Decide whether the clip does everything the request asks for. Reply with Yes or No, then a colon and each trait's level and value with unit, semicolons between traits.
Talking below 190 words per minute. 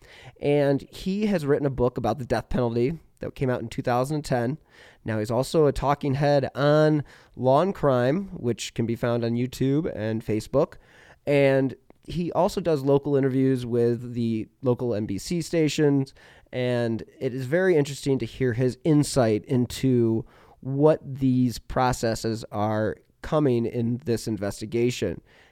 Yes: average, 145 wpm